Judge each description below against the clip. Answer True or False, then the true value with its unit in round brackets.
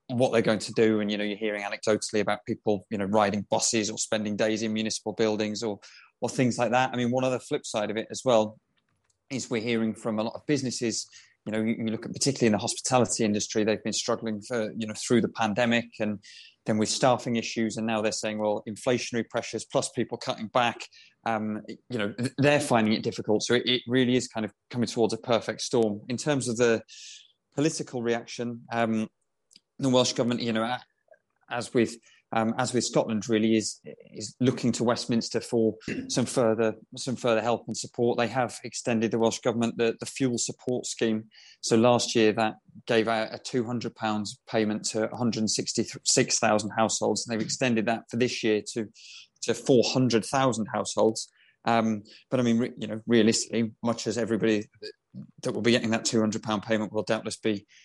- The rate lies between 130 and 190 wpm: False (205 wpm)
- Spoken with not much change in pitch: True (1.8 semitones)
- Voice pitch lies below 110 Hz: False (115 Hz)